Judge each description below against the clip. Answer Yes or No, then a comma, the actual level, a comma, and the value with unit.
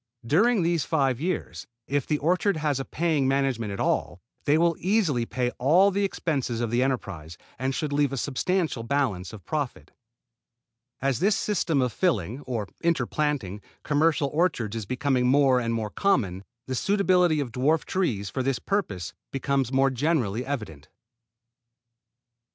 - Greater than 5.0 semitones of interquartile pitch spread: Yes, wide, 5.4 semitones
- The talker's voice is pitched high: No, low, 135 Hz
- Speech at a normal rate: Yes, average, 155 wpm